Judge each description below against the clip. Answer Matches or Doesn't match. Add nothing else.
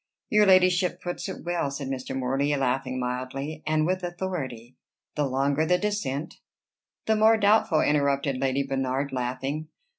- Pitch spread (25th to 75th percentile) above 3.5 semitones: Matches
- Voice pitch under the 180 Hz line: Matches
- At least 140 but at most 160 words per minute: Matches